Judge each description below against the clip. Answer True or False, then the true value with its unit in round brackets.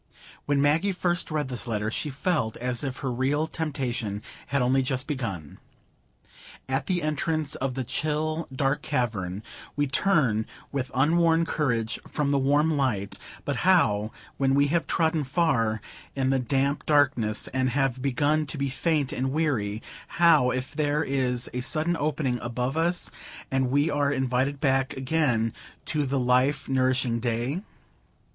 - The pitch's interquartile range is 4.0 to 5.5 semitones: False (3.2 semitones)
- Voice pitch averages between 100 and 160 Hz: True (135 Hz)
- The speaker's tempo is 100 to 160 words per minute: True (155 wpm)